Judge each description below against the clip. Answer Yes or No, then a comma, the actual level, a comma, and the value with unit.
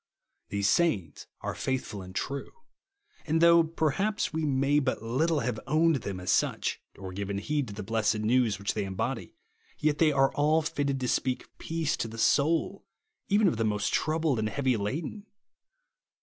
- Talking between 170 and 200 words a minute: Yes, average, 175 wpm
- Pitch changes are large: Yes, wide, 6.6 semitones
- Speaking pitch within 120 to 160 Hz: Yes, low, 135 Hz